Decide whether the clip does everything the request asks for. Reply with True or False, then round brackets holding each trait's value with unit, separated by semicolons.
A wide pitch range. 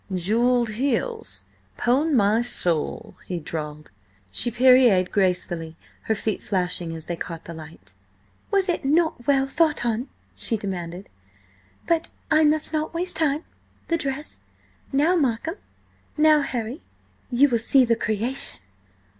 True (8.1 semitones)